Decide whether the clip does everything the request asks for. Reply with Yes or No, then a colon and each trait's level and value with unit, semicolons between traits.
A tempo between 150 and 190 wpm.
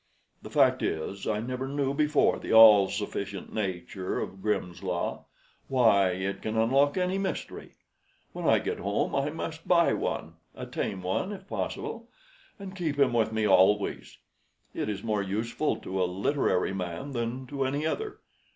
Yes: average, 165 wpm